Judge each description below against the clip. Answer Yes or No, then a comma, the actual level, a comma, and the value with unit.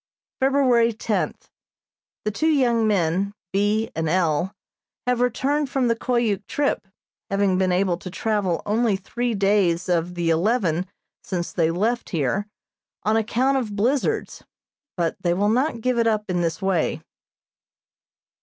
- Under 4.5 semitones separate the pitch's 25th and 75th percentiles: No, average, 4.8 semitones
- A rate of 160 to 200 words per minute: No, average, 145 wpm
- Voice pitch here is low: No, high, 205 Hz